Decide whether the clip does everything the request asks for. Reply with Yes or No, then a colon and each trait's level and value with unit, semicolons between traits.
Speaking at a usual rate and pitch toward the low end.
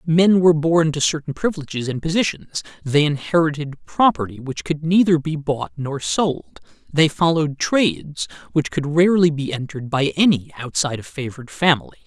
No: average, 160 wpm; medium, 150 Hz